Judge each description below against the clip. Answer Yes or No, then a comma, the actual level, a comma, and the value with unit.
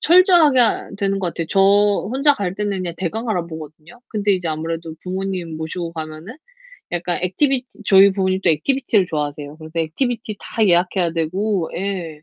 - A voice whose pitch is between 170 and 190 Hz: Yes, medium, 185 Hz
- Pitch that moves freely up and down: No, average, 4.1 semitones